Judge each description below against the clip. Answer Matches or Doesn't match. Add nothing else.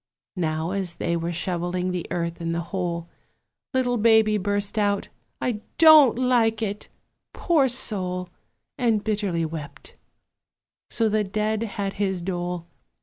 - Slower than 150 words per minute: Matches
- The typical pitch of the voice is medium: Doesn't match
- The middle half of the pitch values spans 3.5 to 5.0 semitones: Matches